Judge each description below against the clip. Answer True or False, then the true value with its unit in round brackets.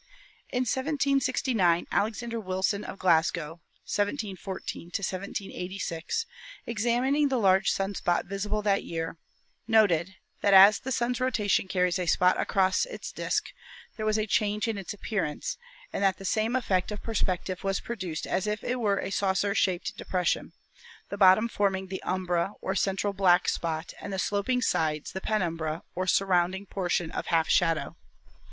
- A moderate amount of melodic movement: True (3.0 semitones)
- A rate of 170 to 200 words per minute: False (155 wpm)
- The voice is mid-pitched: False (195 Hz)